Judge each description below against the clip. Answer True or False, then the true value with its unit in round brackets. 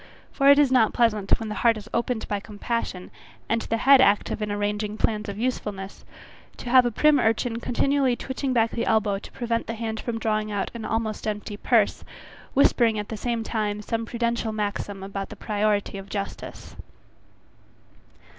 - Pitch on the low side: False (220 Hz)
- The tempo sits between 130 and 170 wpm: False (180 wpm)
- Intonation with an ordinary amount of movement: False (2.2 semitones)